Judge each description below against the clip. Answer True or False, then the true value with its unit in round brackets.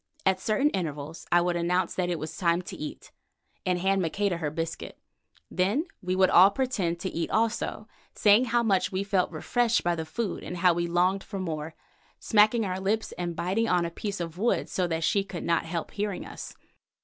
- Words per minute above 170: True (205 wpm)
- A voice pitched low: False (185 Hz)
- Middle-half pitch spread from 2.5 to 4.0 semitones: True (3.2 semitones)